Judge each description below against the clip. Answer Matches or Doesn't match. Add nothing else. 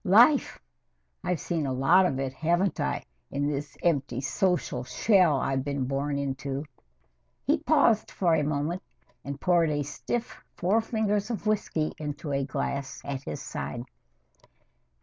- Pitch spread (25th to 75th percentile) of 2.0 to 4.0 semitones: Doesn't match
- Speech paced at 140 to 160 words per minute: Matches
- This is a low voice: Doesn't match